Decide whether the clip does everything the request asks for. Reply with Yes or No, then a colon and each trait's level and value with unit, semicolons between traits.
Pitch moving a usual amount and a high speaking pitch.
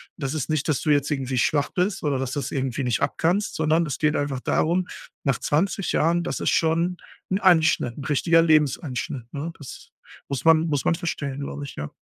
No: average, 3.2 semitones; medium, 150 Hz